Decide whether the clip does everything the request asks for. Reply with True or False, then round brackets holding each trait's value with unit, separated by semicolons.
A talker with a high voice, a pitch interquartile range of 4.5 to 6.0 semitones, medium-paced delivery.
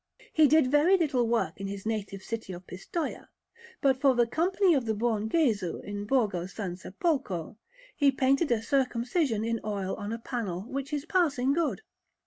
True (235 Hz; 5.6 semitones; 170 wpm)